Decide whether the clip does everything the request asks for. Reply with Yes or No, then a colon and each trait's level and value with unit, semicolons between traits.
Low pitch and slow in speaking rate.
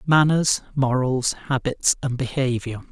Yes: low, 130 Hz; slow, 105 wpm